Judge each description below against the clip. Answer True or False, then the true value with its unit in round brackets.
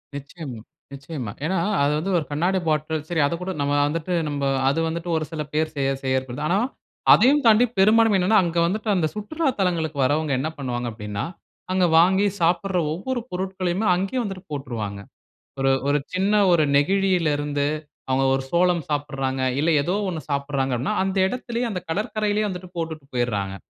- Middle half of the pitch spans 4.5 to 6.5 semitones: True (5.1 semitones)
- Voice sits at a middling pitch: True (165 Hz)